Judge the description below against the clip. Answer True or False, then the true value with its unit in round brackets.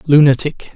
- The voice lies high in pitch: False (145 Hz)